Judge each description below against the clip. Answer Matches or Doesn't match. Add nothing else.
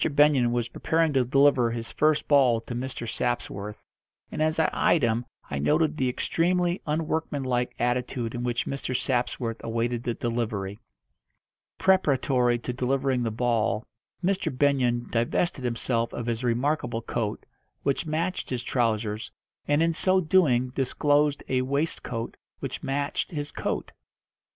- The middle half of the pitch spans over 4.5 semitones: Doesn't match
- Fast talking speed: Doesn't match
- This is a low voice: Matches